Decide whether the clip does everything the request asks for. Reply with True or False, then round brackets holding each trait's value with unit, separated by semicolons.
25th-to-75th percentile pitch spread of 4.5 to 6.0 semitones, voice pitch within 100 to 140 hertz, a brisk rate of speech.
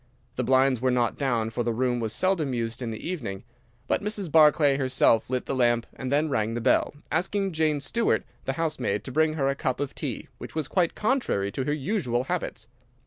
True (4.8 semitones; 135 Hz; 210 wpm)